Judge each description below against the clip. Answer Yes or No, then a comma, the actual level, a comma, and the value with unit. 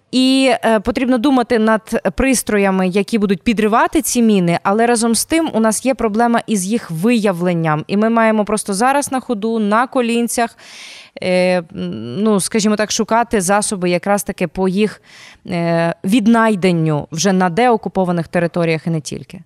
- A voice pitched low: No, high, 215 Hz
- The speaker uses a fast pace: No, average, 145 wpm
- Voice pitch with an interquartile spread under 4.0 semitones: No, average, 4.3 semitones